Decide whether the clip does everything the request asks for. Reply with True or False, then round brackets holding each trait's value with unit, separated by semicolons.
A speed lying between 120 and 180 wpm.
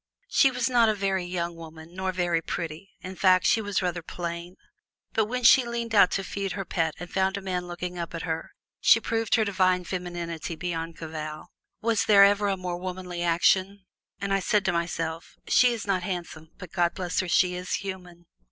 False (205 wpm)